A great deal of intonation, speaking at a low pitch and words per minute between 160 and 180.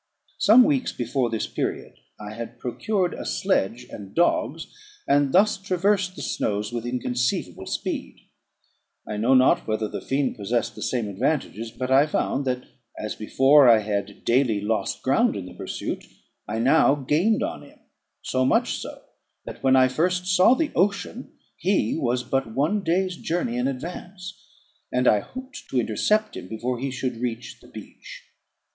Yes: wide, 7.5 semitones; low, 130 Hz; average, 165 wpm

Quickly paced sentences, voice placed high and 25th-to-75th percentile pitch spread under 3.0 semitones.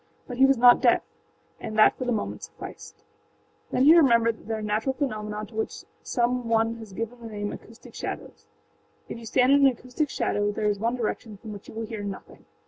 Yes: fast, 220 wpm; high, 230 Hz; narrow, 2.6 semitones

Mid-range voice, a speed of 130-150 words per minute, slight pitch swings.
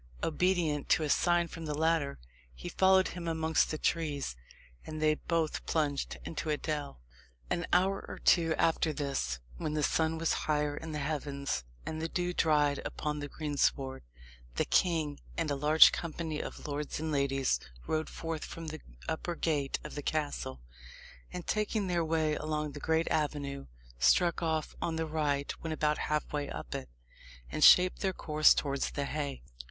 No: medium, 155 Hz; average, 175 wpm; narrow, 2.1 semitones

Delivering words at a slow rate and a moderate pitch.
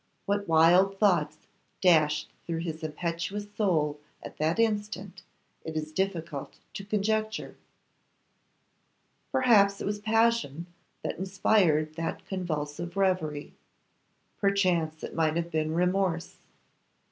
Yes: slow, 110 wpm; medium, 175 Hz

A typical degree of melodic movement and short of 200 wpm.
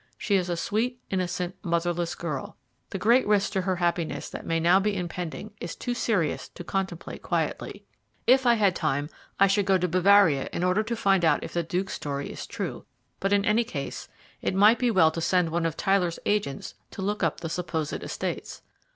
No: average, 3.2 semitones; fast, 205 wpm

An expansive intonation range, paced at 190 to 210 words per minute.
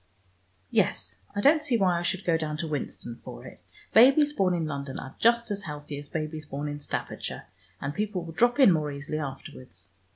Yes: wide, 5.9 semitones; average, 200 wpm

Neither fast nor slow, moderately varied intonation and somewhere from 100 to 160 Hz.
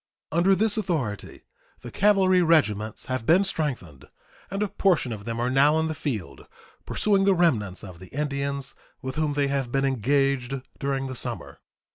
No: average, 170 wpm; wide, 5.9 semitones; medium, 140 Hz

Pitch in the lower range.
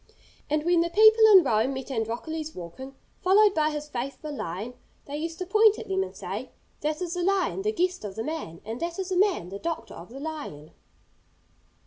No: very high, 310 Hz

